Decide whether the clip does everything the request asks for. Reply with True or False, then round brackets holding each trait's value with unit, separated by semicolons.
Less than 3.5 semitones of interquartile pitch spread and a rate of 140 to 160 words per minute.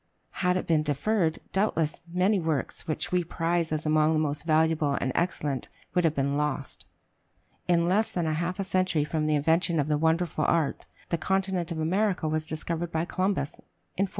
False (2.8 semitones; 185 wpm)